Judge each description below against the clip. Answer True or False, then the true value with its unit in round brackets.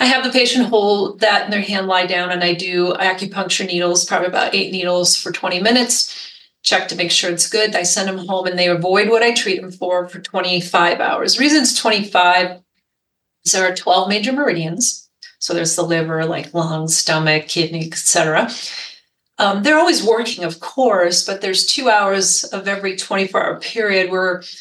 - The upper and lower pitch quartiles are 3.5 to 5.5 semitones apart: False (2.8 semitones)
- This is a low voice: False (185 Hz)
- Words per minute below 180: False (190 wpm)